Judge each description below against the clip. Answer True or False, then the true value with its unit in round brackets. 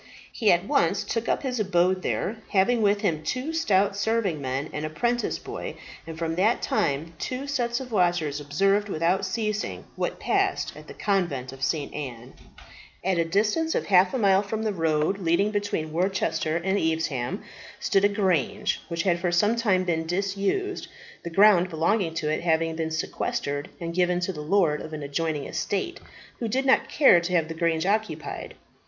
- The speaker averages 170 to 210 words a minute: True (185 wpm)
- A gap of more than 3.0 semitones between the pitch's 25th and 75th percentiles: True (4.3 semitones)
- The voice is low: False (180 Hz)